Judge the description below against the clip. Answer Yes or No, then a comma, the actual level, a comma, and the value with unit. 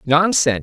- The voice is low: No, medium, 155 Hz